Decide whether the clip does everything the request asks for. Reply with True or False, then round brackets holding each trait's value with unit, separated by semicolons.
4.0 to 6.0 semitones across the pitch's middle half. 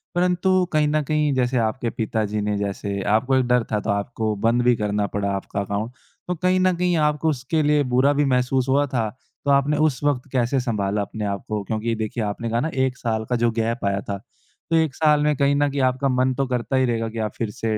True (4.8 semitones)